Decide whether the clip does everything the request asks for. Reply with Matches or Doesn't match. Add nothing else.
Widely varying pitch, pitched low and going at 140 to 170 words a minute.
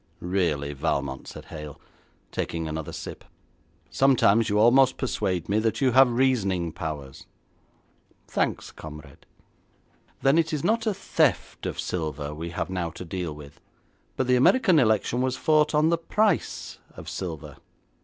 Matches